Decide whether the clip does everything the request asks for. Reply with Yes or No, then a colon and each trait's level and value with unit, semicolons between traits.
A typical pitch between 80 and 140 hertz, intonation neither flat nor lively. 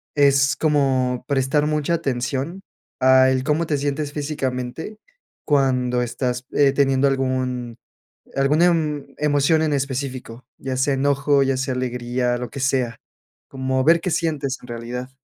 No: low, 135 Hz; narrow, 2.3 semitones